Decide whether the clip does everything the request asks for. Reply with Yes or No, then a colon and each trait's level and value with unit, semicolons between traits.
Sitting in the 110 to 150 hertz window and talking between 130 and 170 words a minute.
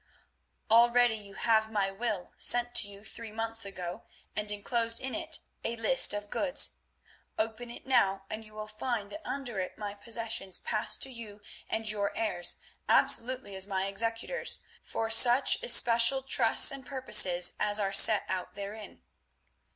No: high, 220 Hz; average, 160 wpm